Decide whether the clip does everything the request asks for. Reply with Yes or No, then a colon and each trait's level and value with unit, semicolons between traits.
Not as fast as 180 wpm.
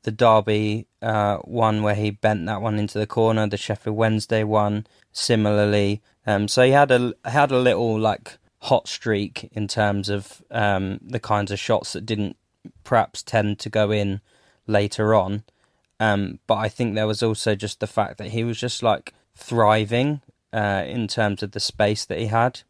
No: average, 190 wpm